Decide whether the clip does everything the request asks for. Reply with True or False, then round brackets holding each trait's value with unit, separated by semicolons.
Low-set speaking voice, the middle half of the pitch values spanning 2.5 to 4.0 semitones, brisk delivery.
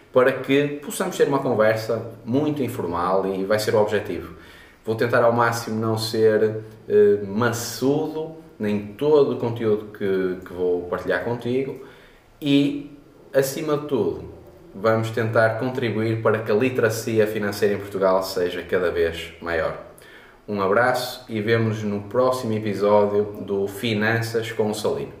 False (110 Hz; 3.5 semitones; 145 wpm)